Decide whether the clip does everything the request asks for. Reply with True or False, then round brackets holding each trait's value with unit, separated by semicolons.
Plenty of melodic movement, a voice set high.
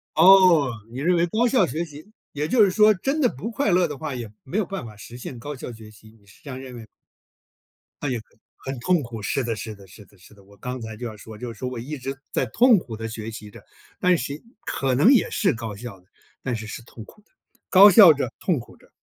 False (8.1 semitones; 130 Hz)